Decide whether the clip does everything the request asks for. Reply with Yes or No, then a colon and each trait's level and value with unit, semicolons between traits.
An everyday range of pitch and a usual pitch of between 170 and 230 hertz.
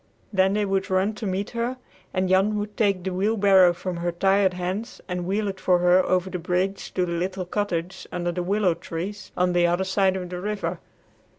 No: narrow, 1.9 semitones; high, 190 Hz